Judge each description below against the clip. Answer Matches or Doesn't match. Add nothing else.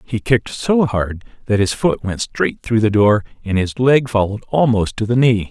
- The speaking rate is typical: Doesn't match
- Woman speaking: Doesn't match